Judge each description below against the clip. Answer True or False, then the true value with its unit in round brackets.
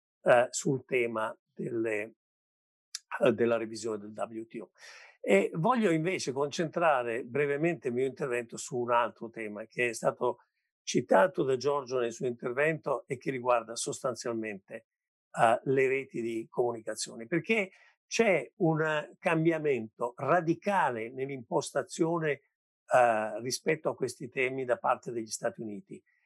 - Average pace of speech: True (125 wpm)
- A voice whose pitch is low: True (130 Hz)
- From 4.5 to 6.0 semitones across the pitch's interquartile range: True (5.5 semitones)